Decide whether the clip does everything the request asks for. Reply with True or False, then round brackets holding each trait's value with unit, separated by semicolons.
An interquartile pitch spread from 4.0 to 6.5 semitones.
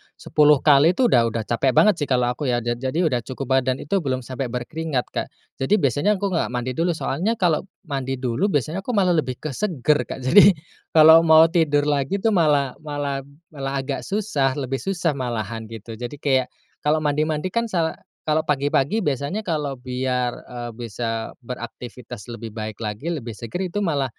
True (4.7 semitones)